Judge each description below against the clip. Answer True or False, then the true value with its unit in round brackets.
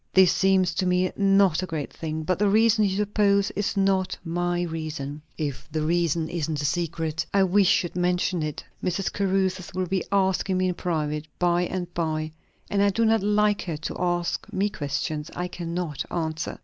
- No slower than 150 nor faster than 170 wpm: False (190 wpm)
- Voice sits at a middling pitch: True (180 Hz)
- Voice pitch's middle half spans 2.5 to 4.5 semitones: True (3.2 semitones)